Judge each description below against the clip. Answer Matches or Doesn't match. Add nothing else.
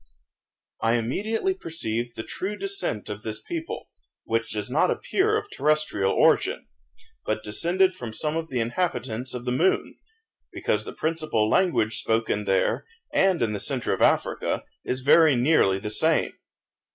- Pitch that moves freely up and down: Matches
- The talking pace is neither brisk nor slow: Matches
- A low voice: Matches